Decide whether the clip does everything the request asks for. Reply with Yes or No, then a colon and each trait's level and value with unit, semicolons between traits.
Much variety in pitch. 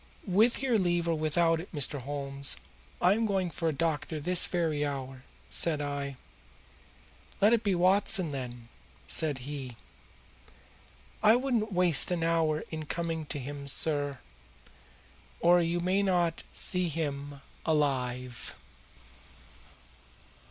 No: average, 3.9 semitones